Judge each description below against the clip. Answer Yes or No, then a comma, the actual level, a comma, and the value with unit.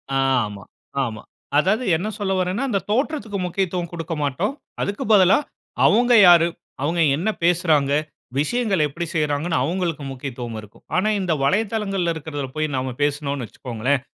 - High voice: No, medium, 170 Hz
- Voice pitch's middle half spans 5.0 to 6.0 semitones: Yes, wide, 5.6 semitones